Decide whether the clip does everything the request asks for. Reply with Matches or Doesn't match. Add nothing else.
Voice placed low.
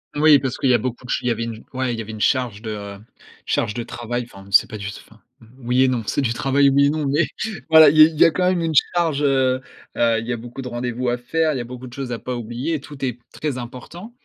Matches